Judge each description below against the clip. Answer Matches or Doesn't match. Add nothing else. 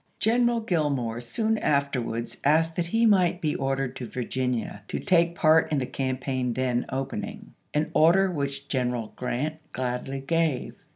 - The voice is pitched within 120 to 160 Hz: Matches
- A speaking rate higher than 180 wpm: Doesn't match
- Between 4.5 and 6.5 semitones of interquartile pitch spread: Matches